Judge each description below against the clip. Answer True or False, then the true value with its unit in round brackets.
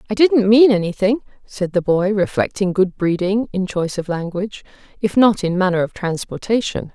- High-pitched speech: True (195 Hz)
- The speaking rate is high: False (175 wpm)